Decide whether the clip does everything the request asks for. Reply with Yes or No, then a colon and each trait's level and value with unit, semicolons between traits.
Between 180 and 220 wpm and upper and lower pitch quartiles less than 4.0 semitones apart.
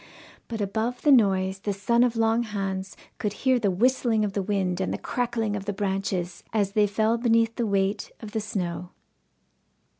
Yes: average, 185 wpm; average, 2.8 semitones